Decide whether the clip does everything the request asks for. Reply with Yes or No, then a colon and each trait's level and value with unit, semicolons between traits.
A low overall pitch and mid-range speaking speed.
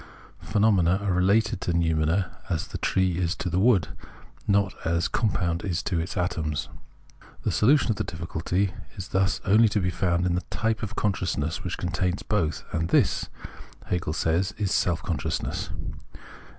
Yes: very low, 90 Hz; average, 165 wpm